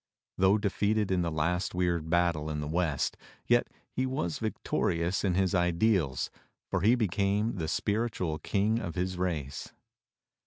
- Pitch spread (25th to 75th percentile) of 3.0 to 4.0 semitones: Yes, average, 3.6 semitones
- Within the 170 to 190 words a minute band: No, average, 155 wpm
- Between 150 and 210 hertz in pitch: No, very low, 90 Hz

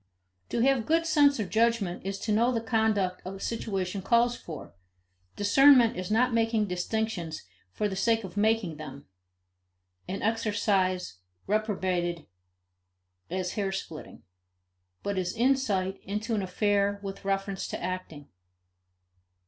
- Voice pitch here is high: Yes, high, 205 Hz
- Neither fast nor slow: No, slow, 130 wpm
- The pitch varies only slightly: No, average, 3.5 semitones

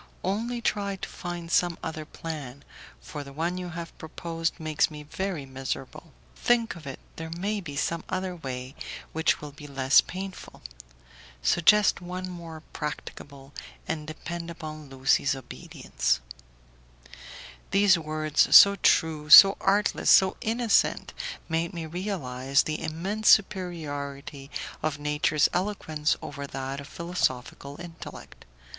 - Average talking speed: No, slow, 130 wpm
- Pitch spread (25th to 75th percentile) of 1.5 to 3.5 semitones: No, average, 4.0 semitones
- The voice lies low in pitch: No, medium, 160 Hz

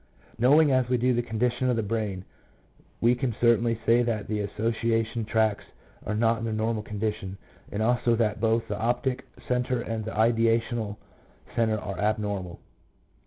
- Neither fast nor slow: Yes, average, 165 wpm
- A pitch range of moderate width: No, narrow, 1.9 semitones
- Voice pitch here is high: No, low, 115 Hz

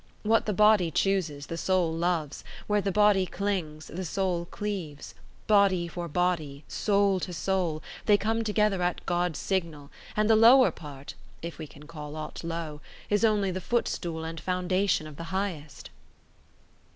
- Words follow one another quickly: No, average, 160 wpm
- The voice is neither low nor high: Yes, medium, 180 Hz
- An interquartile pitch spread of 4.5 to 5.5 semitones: No, average, 3.8 semitones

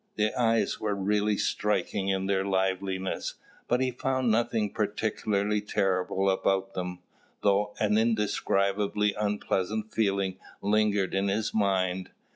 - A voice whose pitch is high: No, low, 100 Hz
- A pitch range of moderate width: No, narrow, 1.8 semitones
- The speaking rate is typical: No, slow, 120 wpm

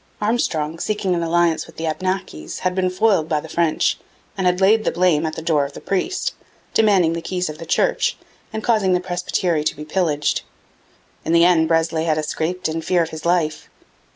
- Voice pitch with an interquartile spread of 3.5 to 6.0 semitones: No, average, 2.7 semitones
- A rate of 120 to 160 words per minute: No, fast, 205 wpm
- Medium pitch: Yes, medium, 170 Hz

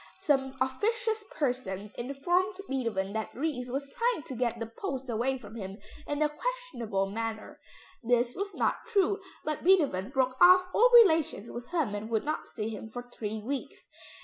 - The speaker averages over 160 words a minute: Yes, average, 170 wpm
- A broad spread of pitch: Yes, wide, 7.3 semitones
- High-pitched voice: Yes, very high, 260 Hz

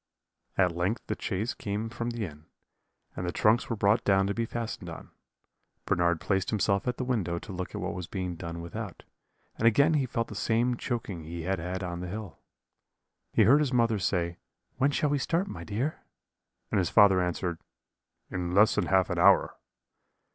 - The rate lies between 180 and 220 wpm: Yes, average, 195 wpm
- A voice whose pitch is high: No, low, 100 Hz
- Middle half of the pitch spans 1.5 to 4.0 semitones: No, average, 4.7 semitones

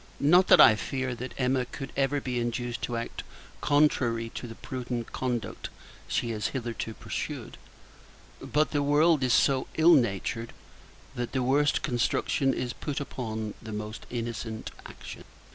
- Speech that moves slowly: No, average, 150 wpm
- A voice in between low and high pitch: No, low, 125 Hz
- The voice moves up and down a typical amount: Yes, average, 3.0 semitones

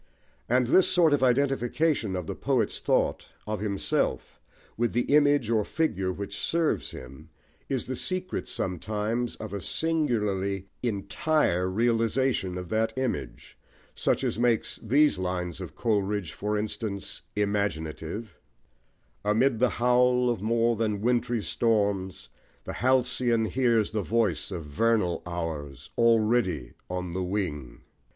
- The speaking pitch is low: Yes, low, 110 Hz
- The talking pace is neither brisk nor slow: No, slow, 130 wpm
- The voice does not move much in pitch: No, average, 4.6 semitones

